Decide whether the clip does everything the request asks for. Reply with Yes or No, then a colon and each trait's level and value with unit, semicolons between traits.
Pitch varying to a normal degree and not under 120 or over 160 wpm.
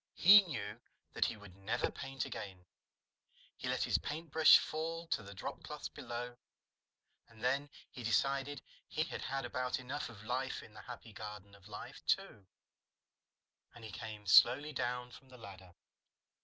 Yes: average, 4.6 semitones; average, 155 wpm